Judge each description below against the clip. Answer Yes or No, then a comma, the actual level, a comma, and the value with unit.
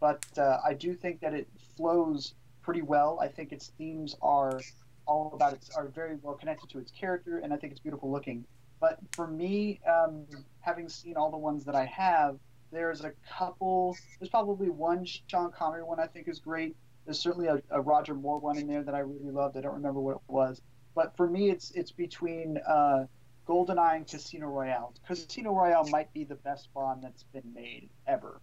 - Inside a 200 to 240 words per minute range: Yes, fast, 205 wpm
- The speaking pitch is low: No, medium, 150 Hz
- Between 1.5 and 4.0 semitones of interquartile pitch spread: Yes, average, 3.6 semitones